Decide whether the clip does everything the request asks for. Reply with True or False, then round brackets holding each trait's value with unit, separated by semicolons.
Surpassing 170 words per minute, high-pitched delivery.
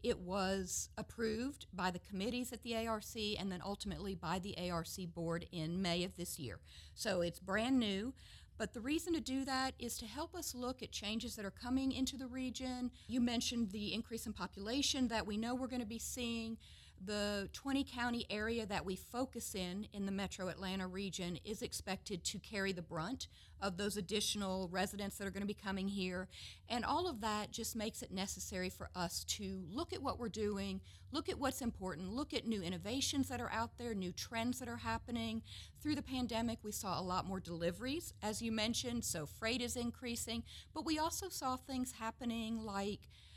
True (200 wpm; 220 Hz)